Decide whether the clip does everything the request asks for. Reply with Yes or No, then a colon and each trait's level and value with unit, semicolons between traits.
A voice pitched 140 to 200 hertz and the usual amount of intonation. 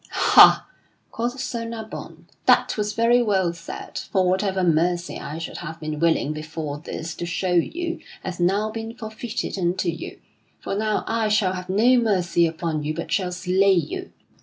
Yes: medium, 185 Hz; average, 4.5 semitones